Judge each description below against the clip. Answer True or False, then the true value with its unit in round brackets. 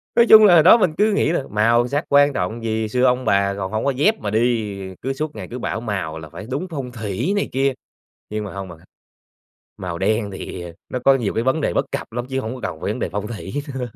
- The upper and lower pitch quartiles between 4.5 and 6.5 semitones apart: True (5.2 semitones)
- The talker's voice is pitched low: True (120 Hz)